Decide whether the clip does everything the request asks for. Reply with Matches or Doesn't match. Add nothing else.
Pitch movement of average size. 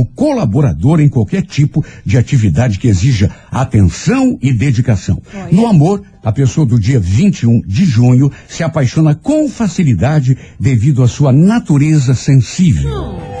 Matches